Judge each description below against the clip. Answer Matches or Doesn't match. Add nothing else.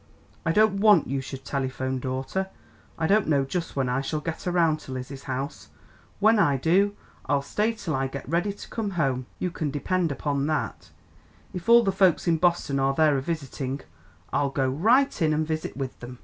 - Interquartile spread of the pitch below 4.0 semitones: Doesn't match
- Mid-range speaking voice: Matches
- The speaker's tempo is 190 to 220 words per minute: Matches